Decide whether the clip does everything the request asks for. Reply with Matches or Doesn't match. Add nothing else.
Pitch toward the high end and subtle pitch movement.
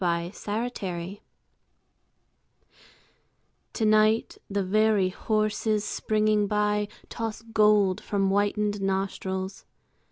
Matches